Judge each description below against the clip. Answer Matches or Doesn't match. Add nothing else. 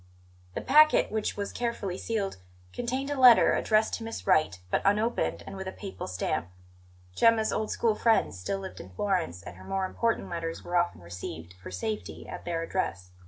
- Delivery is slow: Doesn't match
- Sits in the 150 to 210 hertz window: Matches